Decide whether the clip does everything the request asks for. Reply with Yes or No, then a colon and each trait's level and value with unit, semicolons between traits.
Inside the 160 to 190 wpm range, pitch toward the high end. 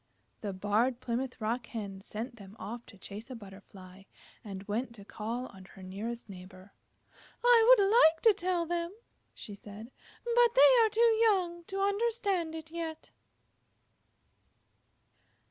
No: average, 145 wpm; high, 245 Hz